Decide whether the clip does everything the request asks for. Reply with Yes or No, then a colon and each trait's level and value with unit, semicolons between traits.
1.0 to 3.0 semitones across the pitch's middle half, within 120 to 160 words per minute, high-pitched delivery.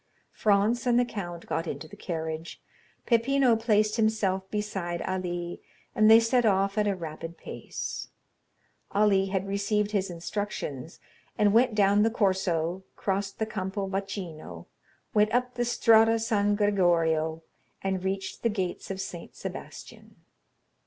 No: average, 3.4 semitones; average, 140 wpm; high, 200 Hz